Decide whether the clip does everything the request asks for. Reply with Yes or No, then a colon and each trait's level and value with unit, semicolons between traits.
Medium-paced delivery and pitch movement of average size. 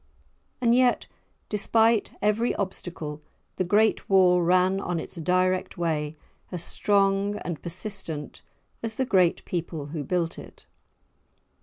No: slow, 125 wpm; average, 3.5 semitones